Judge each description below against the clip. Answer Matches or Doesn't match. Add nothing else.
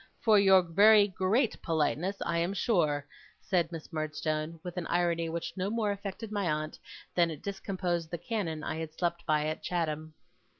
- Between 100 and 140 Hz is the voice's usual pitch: Doesn't match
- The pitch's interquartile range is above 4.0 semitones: Doesn't match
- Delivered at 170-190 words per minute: Matches